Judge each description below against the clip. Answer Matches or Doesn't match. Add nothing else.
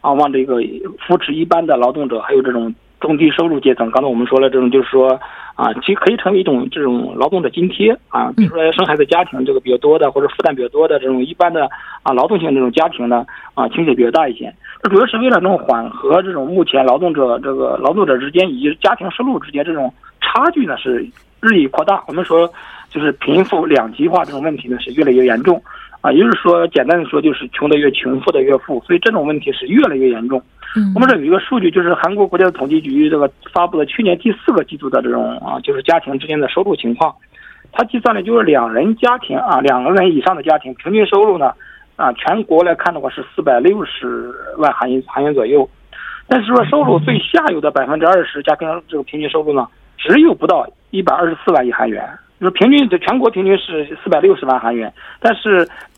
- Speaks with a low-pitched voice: Doesn't match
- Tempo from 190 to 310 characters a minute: Doesn't match